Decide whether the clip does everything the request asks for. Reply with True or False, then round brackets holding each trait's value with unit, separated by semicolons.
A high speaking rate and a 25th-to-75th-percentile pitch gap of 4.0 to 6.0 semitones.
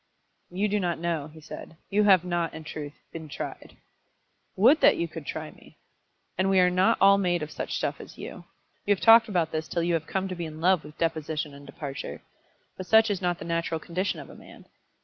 False (225 wpm; 3.1 semitones)